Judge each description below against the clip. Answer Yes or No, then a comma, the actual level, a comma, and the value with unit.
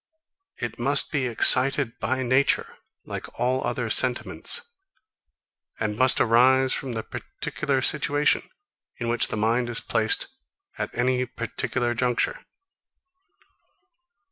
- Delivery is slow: Yes, slow, 115 wpm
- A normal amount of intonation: No, narrow, 1.9 semitones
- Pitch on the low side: Yes, low, 125 Hz